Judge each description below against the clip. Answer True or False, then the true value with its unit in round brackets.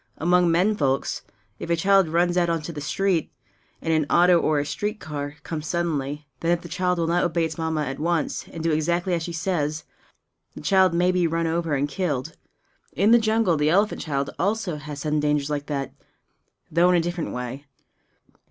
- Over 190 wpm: True (200 wpm)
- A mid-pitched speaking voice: True (165 Hz)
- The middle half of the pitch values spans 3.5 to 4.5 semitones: False (3.0 semitones)